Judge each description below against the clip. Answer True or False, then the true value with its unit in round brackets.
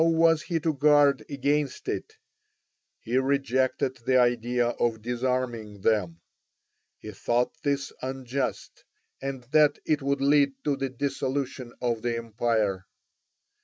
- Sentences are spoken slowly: True (130 wpm)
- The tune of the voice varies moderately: True (3.1 semitones)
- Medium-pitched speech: False (130 Hz)